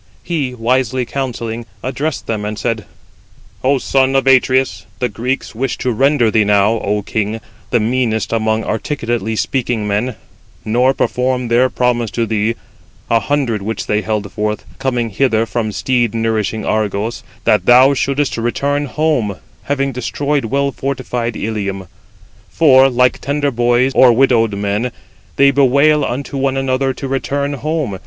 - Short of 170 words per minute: Yes, average, 145 wpm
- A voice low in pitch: Yes, low, 120 Hz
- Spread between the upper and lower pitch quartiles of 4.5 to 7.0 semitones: No, average, 3.5 semitones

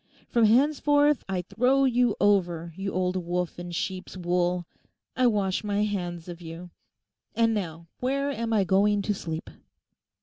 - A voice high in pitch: Yes, high, 195 Hz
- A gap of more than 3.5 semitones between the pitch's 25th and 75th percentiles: Yes, average, 4.8 semitones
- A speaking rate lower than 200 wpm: Yes, average, 155 wpm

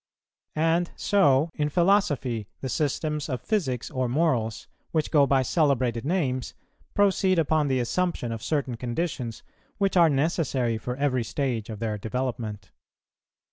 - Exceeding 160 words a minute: No, average, 140 wpm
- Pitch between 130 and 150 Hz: Yes, low, 135 Hz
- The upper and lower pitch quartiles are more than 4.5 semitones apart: Yes, average, 5.2 semitones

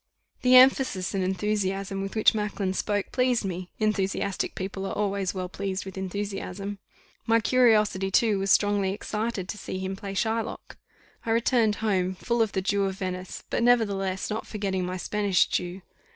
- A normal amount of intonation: No, narrow, 2.2 semitones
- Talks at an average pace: Yes, average, 165 wpm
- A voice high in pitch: Yes, high, 200 Hz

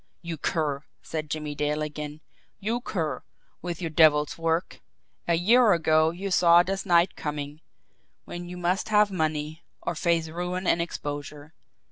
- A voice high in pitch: No, medium, 165 Hz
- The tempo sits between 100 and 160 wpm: Yes, average, 150 wpm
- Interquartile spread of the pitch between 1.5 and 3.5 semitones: Yes, average, 2.8 semitones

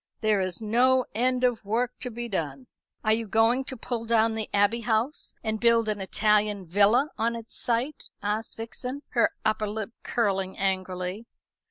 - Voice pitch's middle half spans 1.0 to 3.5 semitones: Yes, narrow, 2.6 semitones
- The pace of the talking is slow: No, average, 170 wpm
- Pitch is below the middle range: No, high, 220 Hz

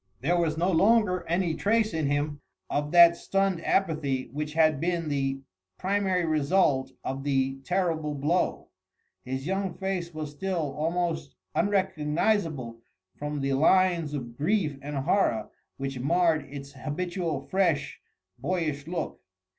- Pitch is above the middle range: No, medium, 160 Hz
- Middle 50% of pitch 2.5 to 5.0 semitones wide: Yes, average, 4.2 semitones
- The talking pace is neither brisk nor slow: No, slow, 130 wpm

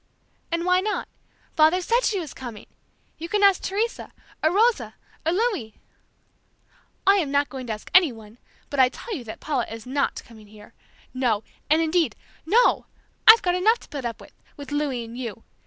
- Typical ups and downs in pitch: No, wide, 7.5 semitones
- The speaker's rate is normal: Yes, average, 185 wpm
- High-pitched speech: Yes, very high, 300 Hz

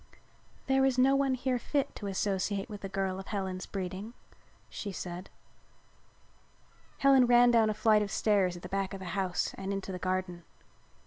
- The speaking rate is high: No, average, 180 wpm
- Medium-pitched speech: No, high, 200 Hz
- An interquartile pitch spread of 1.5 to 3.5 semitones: No, average, 4.3 semitones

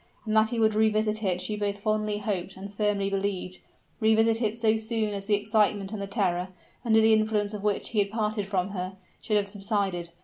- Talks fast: Yes, fast, 210 wpm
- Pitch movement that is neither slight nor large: No, narrow, 1.7 semitones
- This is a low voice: No, high, 210 Hz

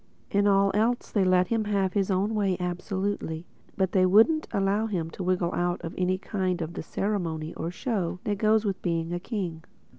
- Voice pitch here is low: No, high, 190 Hz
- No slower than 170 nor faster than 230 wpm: Yes, average, 190 wpm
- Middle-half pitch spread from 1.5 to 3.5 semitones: Yes, narrow, 2.6 semitones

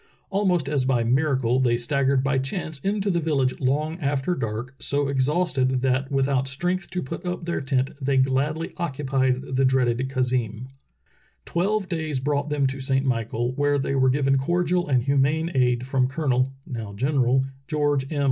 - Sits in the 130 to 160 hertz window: Yes, low, 135 Hz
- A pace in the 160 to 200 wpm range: Yes, average, 170 wpm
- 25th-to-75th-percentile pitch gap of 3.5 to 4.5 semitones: No, average, 2.7 semitones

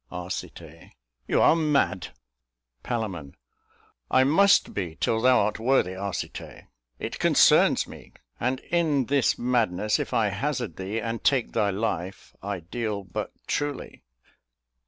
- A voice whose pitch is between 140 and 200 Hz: No, low, 115 Hz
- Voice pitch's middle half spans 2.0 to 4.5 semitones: No, average, 5.3 semitones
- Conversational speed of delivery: No, slow, 130 wpm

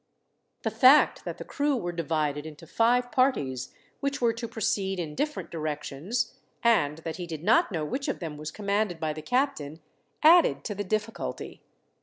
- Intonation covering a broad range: Yes, wide, 7.8 semitones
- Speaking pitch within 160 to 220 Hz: Yes, high, 190 Hz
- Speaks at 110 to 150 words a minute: No, average, 175 wpm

